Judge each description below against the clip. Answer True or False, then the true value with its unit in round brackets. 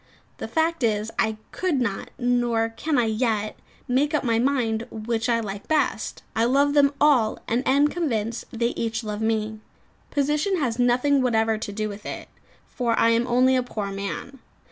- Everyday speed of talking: True (180 wpm)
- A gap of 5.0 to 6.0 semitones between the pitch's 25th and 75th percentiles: False (3.8 semitones)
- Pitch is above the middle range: True (235 Hz)